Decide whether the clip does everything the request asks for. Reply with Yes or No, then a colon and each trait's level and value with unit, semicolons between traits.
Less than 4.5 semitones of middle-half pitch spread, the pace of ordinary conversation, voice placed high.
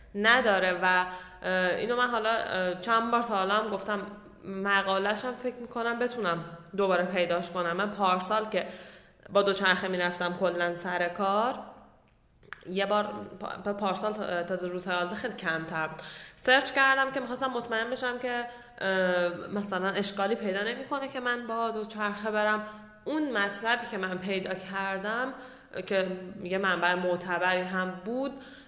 Yes: average, 4.1 semitones; average, 135 wpm; high, 200 Hz